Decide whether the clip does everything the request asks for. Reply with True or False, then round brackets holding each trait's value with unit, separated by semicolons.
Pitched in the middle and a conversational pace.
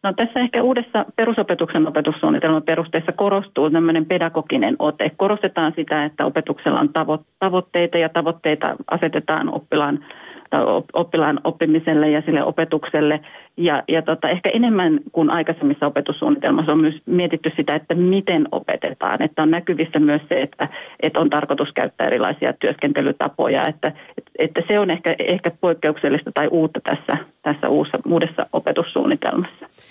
True (165 Hz; 135 wpm)